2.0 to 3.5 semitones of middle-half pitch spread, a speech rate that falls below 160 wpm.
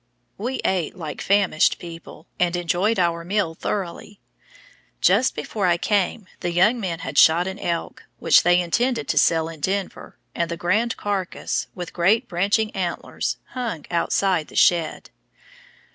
Yes: average, 3.2 semitones; average, 150 wpm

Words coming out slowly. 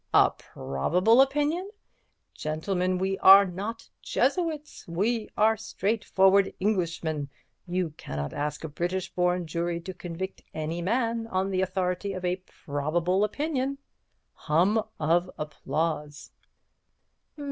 Yes: slow, 115 wpm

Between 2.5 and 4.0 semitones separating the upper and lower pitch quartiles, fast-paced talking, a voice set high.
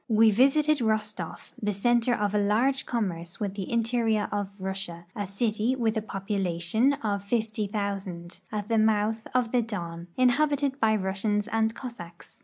No: average, 2.9 semitones; average, 155 wpm; high, 215 Hz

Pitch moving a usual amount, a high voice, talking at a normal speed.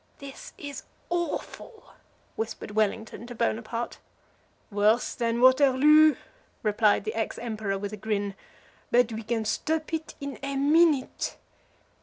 No: average, 4.6 semitones; high, 235 Hz; slow, 125 wpm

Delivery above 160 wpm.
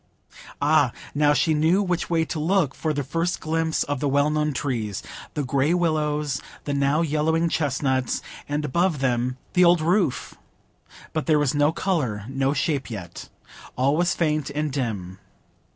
No: average, 155 wpm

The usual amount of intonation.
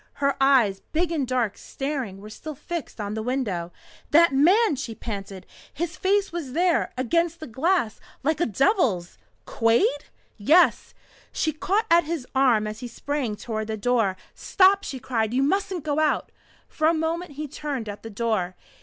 No: wide, 6.8 semitones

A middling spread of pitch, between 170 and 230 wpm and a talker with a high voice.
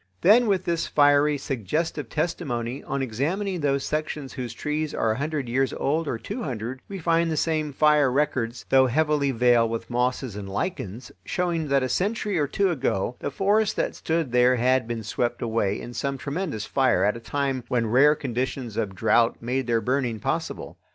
No: average, 4.5 semitones; average, 185 wpm; low, 135 Hz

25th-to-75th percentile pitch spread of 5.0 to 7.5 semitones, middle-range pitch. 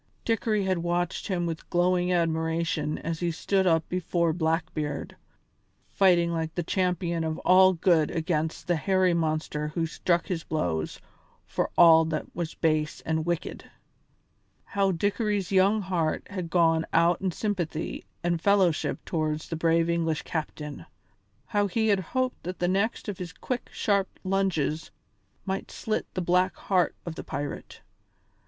No: average, 2.7 semitones; medium, 170 Hz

